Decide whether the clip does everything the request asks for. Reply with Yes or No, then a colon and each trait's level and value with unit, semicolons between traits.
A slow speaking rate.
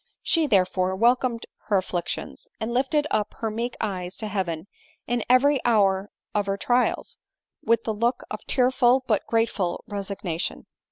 No: average, 150 wpm